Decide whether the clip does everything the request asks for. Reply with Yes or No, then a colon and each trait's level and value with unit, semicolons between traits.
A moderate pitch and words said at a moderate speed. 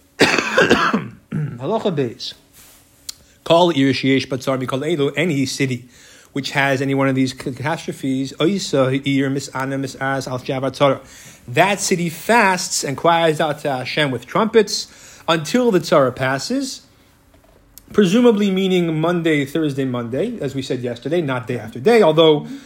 No: medium, 145 Hz; slow, 115 wpm